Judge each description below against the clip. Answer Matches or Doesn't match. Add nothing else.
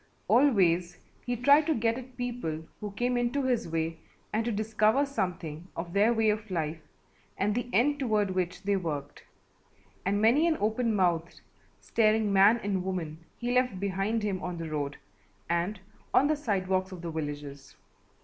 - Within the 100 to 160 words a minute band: Doesn't match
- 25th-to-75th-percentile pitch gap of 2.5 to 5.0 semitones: Doesn't match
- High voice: Matches